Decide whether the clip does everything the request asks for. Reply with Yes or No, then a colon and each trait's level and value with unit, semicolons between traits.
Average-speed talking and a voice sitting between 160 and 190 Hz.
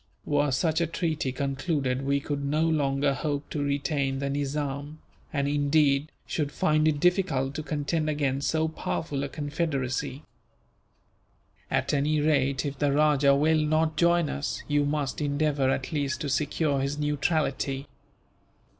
No: average, 145 wpm; medium, 145 Hz